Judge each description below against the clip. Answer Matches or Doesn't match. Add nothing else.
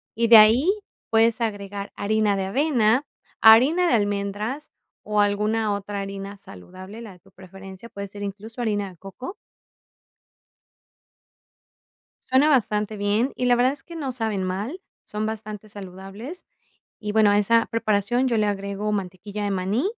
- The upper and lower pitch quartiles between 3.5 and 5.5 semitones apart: Doesn't match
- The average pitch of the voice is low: Doesn't match